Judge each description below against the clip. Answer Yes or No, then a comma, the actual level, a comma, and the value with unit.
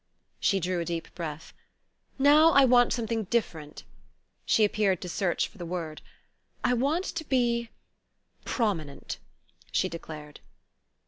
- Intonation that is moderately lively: No, wide, 6.5 semitones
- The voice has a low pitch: No, high, 205 Hz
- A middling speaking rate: No, slow, 130 wpm